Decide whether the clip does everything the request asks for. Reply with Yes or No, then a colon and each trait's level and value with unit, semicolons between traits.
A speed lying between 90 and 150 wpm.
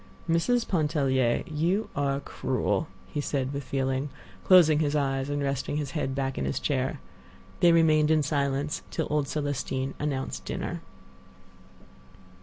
Yes: average, 140 wpm